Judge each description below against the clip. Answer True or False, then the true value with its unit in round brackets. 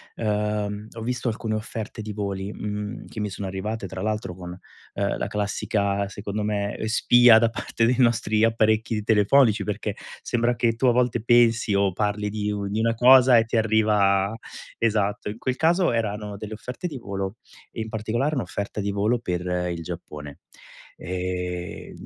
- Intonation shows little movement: True (2.2 semitones)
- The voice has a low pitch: True (105 Hz)